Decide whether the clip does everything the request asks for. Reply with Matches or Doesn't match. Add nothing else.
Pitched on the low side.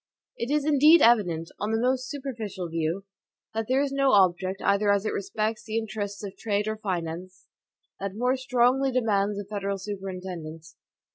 Doesn't match